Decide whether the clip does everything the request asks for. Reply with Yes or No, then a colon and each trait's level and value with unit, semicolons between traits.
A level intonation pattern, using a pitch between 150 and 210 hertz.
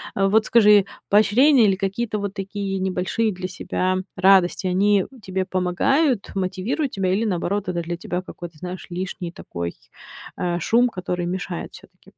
Yes: narrow, 2.3 semitones; high, 190 Hz